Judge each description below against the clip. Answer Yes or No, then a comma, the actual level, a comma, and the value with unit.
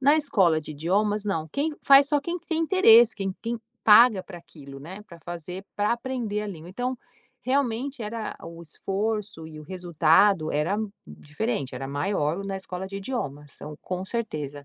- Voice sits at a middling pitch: No, high, 195 Hz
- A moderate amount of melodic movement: No, wide, 6.4 semitones